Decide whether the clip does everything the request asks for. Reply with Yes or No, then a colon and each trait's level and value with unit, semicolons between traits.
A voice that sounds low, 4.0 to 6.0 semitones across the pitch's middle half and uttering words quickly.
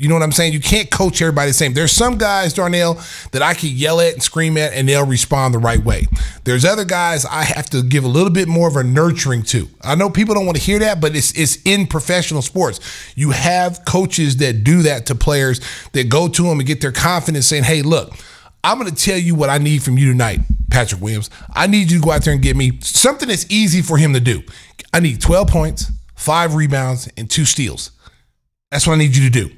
No: medium, 150 Hz; average, 4.6 semitones; fast, 250 wpm